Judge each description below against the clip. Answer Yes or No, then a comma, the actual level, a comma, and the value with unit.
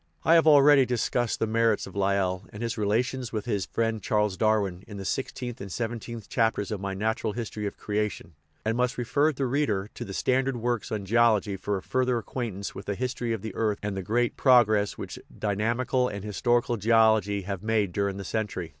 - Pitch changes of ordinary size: Yes, average, 3.0 semitones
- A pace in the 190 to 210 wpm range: Yes, fast, 205 wpm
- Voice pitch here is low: Yes, low, 110 Hz